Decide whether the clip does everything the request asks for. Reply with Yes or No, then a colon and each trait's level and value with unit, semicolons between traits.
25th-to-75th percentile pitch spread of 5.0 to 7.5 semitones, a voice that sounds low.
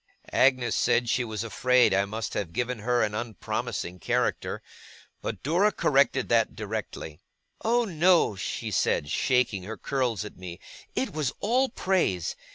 Yes: wide, 5.5 semitones; low, 120 Hz